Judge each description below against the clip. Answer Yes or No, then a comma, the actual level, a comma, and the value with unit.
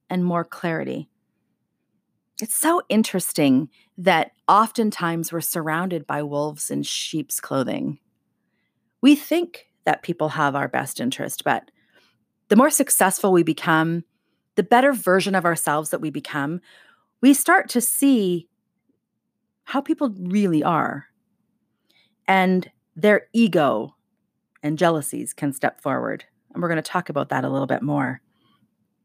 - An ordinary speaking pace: No, slow, 130 wpm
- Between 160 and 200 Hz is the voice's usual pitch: Yes, medium, 185 Hz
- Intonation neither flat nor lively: No, wide, 6.1 semitones